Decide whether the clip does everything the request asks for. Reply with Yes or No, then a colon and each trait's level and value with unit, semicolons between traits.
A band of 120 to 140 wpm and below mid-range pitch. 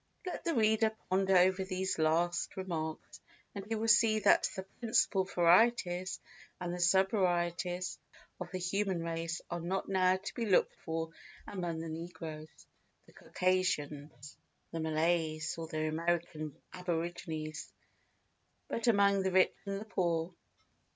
No: slow, 135 wpm; medium, 180 Hz